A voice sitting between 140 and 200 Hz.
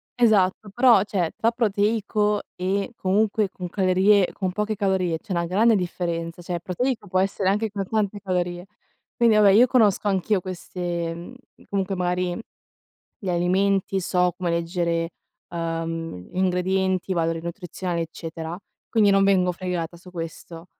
Yes: medium, 185 Hz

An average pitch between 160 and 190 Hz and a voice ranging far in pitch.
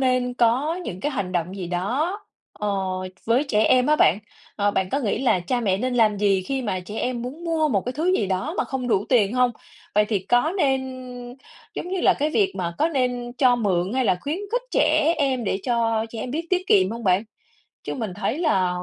No: high, 245 Hz; wide, 5.9 semitones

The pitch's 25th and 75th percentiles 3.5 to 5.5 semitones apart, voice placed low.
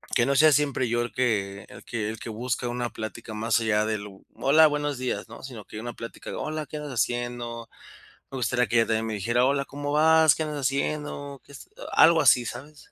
Yes: average, 3.9 semitones; low, 125 Hz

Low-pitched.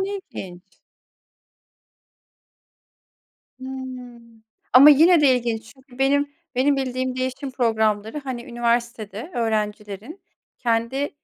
No: very high, 250 Hz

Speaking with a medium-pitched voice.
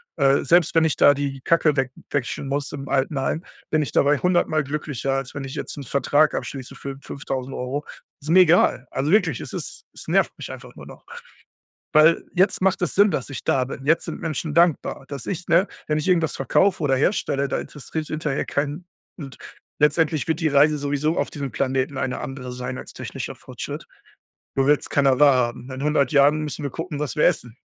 Yes: medium, 145 Hz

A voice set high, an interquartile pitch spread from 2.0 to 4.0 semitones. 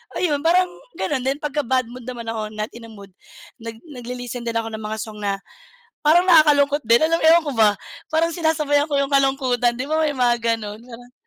No: very high, 255 Hz; average, 4.6 semitones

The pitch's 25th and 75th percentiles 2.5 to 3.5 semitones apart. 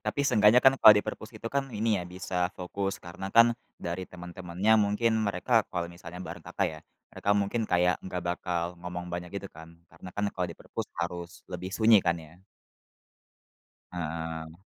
Yes: average, 2.9 semitones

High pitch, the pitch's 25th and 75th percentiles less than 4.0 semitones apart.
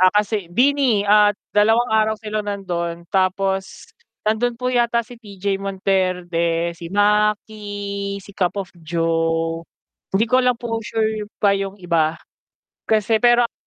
Yes: high, 205 Hz; average, 3.1 semitones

